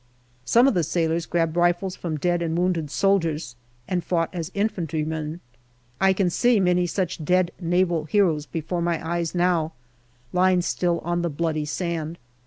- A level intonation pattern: Yes, narrow, 1.9 semitones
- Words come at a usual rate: Yes, average, 160 wpm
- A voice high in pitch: No, medium, 170 Hz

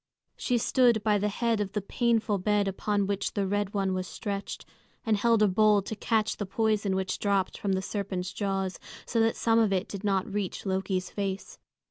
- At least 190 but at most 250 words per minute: Yes, average, 200 wpm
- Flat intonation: Yes, narrow, 2.0 semitones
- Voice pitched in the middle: No, high, 205 Hz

